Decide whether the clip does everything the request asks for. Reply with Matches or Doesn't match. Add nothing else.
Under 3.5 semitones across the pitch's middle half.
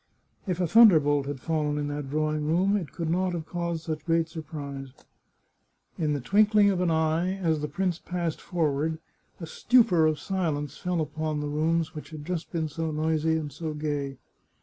Matches